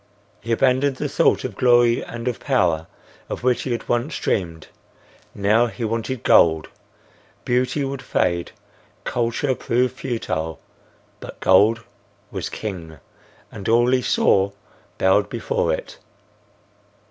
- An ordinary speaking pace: No, slow, 125 wpm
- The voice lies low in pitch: Yes, low, 115 Hz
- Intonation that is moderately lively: Yes, average, 4.3 semitones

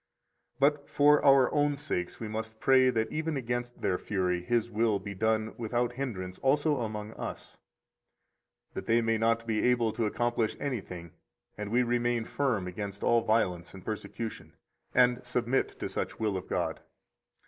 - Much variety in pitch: No, average, 2.8 semitones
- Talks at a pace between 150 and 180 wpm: Yes, average, 160 wpm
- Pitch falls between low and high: No, low, 115 Hz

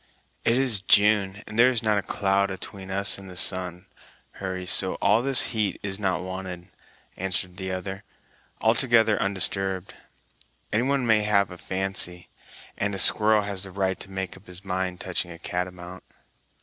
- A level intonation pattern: Yes, narrow, 2.2 semitones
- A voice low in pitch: Yes, very low, 95 Hz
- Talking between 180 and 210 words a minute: No, average, 170 wpm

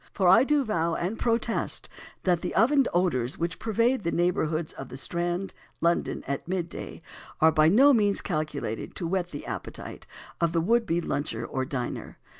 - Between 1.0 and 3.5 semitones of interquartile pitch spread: No, average, 4.9 semitones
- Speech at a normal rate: Yes, average, 175 wpm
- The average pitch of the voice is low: No, medium, 175 Hz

